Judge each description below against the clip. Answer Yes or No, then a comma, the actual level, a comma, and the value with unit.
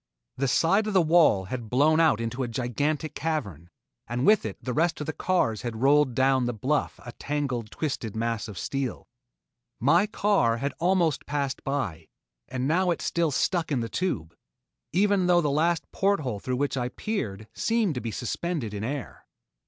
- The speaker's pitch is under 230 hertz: Yes, medium, 140 Hz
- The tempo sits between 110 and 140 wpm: No, average, 185 wpm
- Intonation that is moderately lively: No, wide, 6.0 semitones